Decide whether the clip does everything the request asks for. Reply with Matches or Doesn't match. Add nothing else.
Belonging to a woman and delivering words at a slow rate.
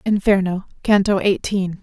Matches